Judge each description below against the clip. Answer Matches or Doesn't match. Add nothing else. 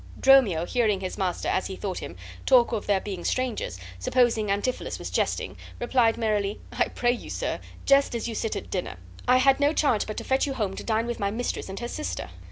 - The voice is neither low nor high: Doesn't match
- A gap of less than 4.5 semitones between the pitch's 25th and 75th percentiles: Matches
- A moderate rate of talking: Doesn't match